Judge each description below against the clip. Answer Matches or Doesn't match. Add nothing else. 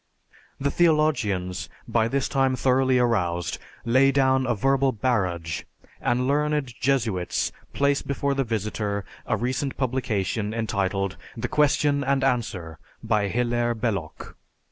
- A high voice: Doesn't match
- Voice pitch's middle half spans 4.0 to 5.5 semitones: Matches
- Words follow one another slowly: Matches